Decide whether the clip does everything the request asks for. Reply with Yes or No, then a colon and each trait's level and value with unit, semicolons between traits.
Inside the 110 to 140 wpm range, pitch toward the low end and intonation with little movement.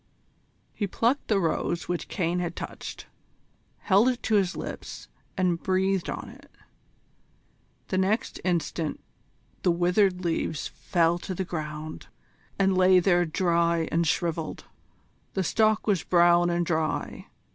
No: slow, 135 wpm; medium, 175 Hz; narrow, 2.1 semitones